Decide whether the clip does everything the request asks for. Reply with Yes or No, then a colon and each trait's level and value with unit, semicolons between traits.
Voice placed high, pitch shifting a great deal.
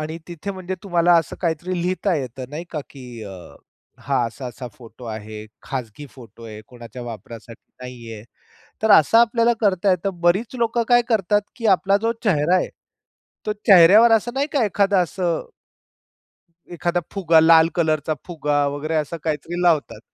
No: medium, 165 Hz; wide, 6.9 semitones